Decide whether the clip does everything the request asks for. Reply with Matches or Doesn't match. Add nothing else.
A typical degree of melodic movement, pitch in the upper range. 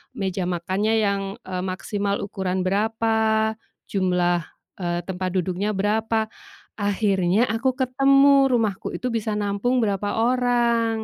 Matches